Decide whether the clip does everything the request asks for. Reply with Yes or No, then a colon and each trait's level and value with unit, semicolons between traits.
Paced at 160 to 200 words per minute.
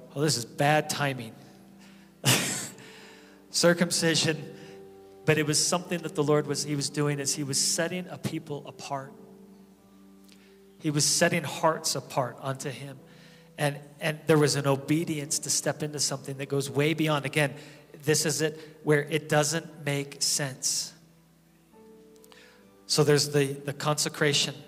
No: average, 145 wpm